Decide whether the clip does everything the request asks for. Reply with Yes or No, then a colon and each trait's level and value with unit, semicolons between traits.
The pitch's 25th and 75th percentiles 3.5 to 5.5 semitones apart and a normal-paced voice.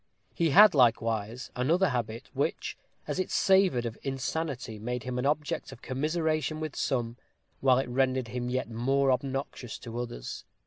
Yes: average, 4.0 semitones; average, 160 wpm